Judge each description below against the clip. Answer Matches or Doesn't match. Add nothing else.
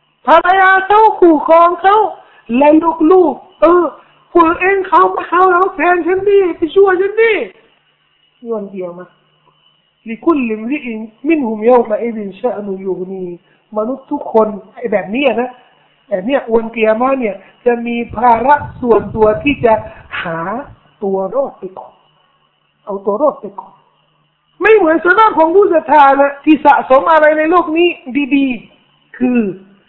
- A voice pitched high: Matches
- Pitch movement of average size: Doesn't match